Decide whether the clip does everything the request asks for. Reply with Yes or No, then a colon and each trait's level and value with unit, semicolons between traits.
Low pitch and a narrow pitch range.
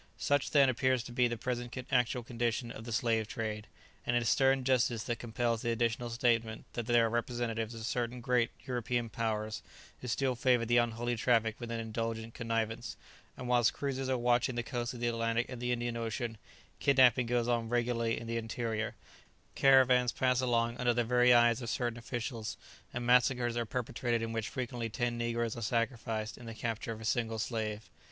Yes: low, 120 Hz; narrow, 1.3 semitones